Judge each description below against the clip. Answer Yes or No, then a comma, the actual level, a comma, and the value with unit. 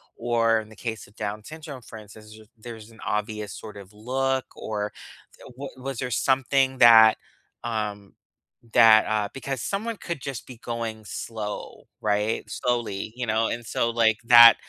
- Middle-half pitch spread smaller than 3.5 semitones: Yes, average, 2.8 semitones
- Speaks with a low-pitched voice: Yes, low, 115 Hz